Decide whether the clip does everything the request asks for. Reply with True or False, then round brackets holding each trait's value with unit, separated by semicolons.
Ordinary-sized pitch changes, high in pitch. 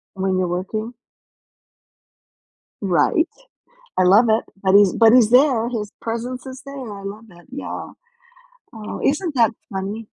True (4.1 semitones; 220 Hz)